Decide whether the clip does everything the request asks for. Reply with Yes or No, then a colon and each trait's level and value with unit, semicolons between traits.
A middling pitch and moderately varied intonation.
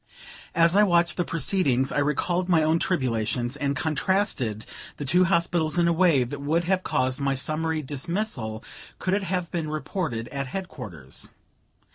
Yes: medium, 155 Hz; average, 5.0 semitones